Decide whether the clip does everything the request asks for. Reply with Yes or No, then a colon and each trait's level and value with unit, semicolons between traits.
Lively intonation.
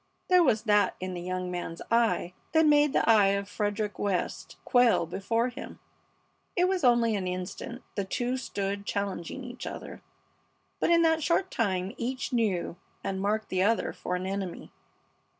No: average, 4.7 semitones